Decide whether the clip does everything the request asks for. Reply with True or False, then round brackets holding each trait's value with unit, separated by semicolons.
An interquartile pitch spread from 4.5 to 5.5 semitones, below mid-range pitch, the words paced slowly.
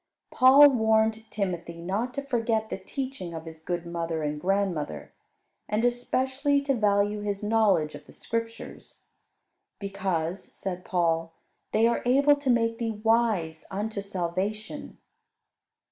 False (5.1 semitones; 210 Hz; 130 wpm)